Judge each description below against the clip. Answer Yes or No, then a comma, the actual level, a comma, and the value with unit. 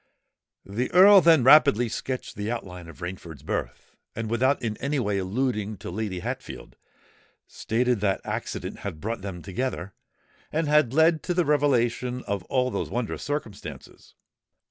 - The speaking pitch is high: No, low, 120 Hz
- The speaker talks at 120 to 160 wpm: Yes, average, 150 wpm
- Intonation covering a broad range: Yes, wide, 5.7 semitones